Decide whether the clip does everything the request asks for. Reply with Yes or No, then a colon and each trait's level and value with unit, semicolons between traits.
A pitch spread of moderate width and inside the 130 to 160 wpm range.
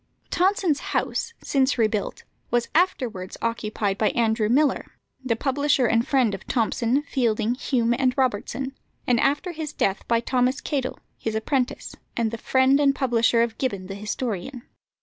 Yes: average, 3.4 semitones; average, 150 wpm